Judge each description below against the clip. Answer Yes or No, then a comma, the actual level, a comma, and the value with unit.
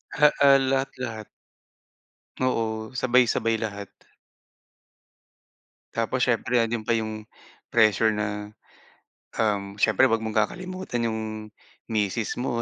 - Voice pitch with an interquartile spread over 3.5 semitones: No, average, 2.8 semitones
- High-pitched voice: No, low, 115 Hz